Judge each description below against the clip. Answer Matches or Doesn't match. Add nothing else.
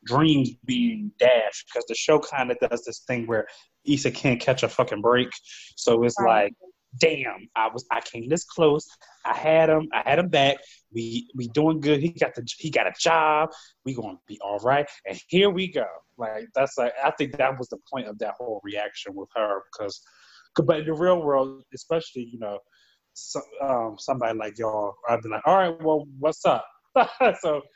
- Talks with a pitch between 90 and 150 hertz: Matches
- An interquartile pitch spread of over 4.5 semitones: Matches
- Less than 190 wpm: Doesn't match